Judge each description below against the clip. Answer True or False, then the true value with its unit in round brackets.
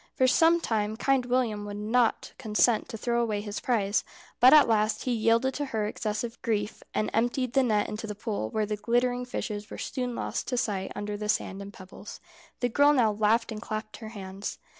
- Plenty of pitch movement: False (2.8 semitones)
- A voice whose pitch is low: False (220 Hz)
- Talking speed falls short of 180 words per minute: False (205 wpm)